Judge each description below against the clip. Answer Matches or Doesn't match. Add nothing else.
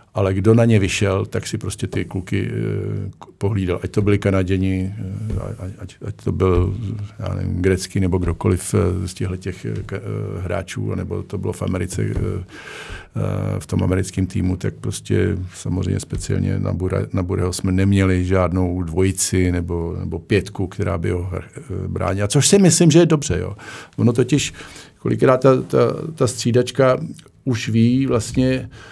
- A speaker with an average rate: Matches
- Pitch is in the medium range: Doesn't match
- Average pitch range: Matches